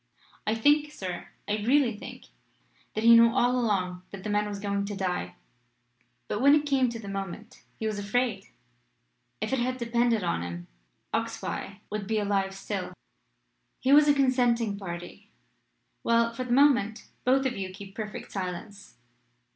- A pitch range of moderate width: Yes, average, 3.9 semitones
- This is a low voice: No, high, 215 Hz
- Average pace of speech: Yes, average, 165 wpm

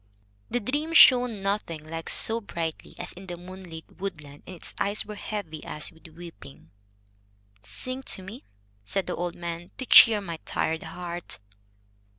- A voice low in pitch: No, medium, 175 Hz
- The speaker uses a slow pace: No, average, 160 wpm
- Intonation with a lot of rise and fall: No, average, 4.3 semitones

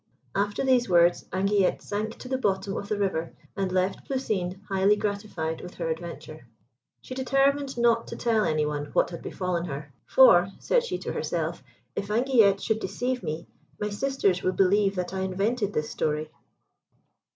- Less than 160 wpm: No, average, 170 wpm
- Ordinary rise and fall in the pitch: Yes, average, 4.5 semitones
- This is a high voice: Yes, high, 195 Hz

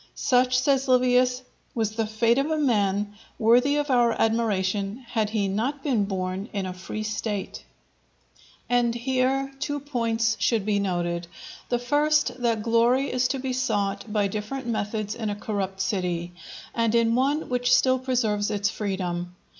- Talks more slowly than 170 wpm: Yes, average, 155 wpm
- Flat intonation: No, average, 3.7 semitones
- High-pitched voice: Yes, high, 230 Hz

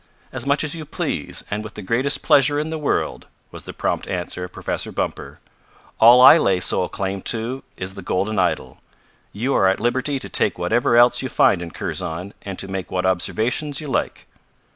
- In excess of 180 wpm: Yes, average, 200 wpm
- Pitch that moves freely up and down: Yes, wide, 6.0 semitones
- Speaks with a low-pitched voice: Yes, low, 110 Hz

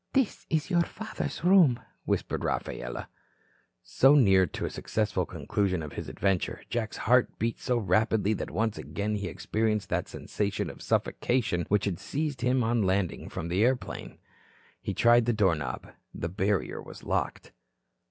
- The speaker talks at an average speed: Yes, average, 160 wpm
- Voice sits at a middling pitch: No, low, 110 Hz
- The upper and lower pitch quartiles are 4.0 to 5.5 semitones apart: Yes, average, 4.4 semitones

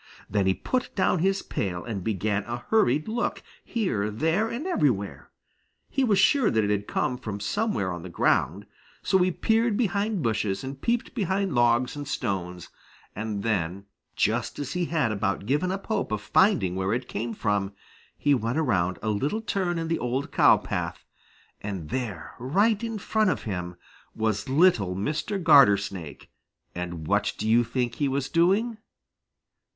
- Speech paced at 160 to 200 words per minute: Yes, average, 170 wpm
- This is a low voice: Yes, low, 125 Hz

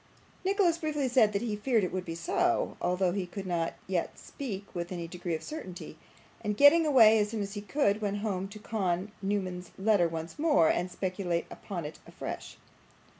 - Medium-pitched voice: No, high, 200 Hz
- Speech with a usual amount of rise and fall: Yes, average, 3.8 semitones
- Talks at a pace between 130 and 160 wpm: No, average, 190 wpm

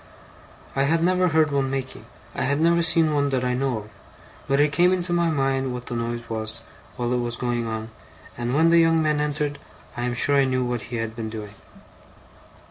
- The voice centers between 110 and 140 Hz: Yes, low, 135 Hz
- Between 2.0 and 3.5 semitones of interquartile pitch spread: No, average, 4.5 semitones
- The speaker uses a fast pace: Yes, fast, 215 wpm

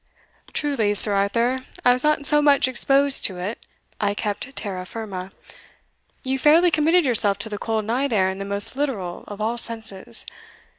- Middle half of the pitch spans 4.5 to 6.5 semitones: Yes, wide, 5.4 semitones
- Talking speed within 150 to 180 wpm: Yes, average, 170 wpm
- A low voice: No, high, 225 Hz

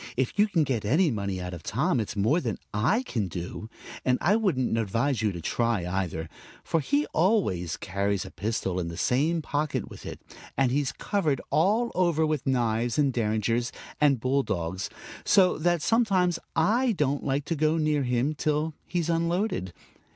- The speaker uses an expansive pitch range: Yes, wide, 7.4 semitones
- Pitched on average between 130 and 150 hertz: Yes, low, 135 Hz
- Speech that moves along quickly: No, average, 180 wpm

